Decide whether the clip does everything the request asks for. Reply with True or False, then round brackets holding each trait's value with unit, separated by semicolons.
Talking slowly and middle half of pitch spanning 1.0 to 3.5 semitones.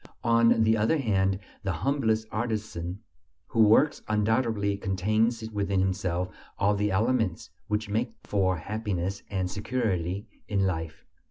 True (125 wpm; 2.9 semitones)